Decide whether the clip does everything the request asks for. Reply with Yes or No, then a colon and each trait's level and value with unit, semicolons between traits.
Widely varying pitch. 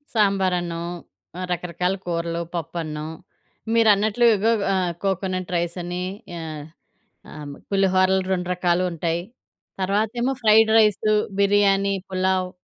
No: narrow, 2.6 semitones